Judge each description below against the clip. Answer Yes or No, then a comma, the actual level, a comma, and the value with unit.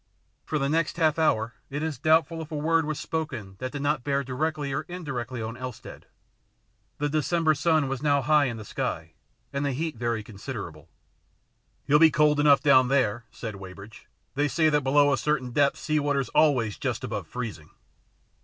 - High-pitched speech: No, medium, 140 Hz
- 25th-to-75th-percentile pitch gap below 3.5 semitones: No, average, 4.0 semitones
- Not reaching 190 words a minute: No, average, 195 wpm